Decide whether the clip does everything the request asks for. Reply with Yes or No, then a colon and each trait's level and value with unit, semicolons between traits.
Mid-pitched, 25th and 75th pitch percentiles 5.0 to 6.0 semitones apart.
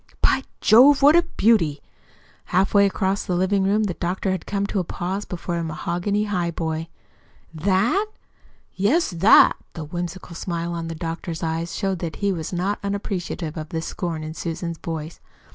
No: medium, 180 Hz; average, 3.3 semitones